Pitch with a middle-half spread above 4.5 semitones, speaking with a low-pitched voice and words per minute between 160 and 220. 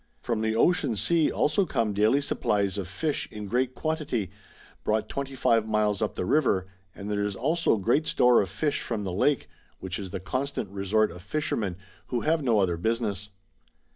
Yes: wide, 5.6 semitones; low, 110 Hz; average, 180 wpm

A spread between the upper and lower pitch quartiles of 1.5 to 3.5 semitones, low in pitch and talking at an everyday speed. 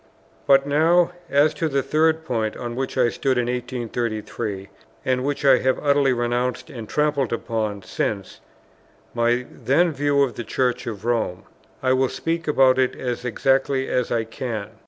Yes: average, 3.0 semitones; low, 130 Hz; average, 165 wpm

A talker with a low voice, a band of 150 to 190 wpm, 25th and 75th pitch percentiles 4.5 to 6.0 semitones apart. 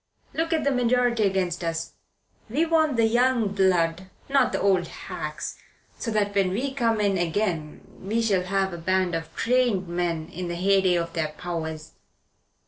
No: high, 190 Hz; average, 170 wpm; average, 5.1 semitones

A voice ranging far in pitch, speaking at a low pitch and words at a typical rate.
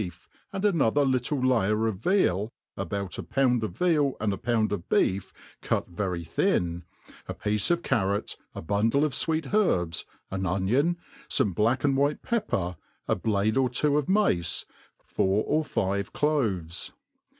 Yes: wide, 6.9 semitones; low, 110 Hz; average, 155 wpm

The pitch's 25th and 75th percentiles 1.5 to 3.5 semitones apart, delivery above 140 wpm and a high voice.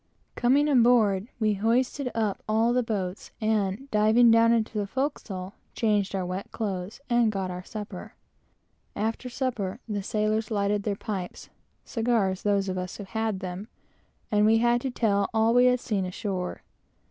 Yes: average, 3.0 semitones; average, 160 wpm; high, 215 Hz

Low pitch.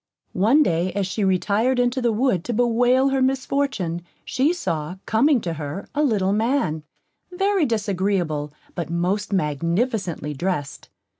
No: high, 205 Hz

